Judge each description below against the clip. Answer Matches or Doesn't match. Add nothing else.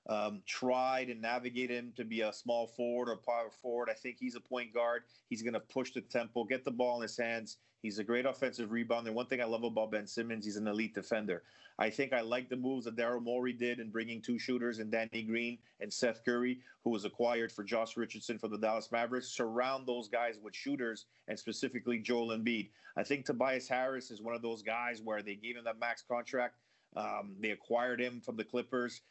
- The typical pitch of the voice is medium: Doesn't match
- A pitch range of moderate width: Doesn't match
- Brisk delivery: Matches